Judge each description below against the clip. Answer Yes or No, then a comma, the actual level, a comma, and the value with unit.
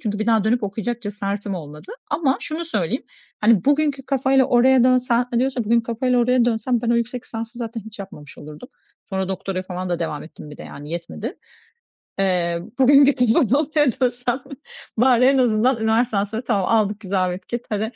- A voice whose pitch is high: Yes, high, 230 Hz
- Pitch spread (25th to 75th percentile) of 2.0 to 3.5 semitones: No, average, 4.3 semitones